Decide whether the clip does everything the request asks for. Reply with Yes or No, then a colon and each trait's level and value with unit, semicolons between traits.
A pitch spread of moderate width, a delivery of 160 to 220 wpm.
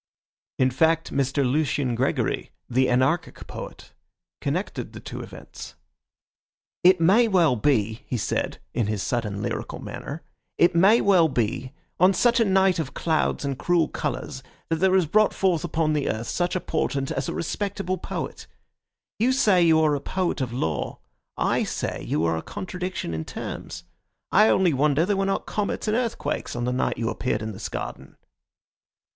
No: wide, 6.6 semitones; average, 175 wpm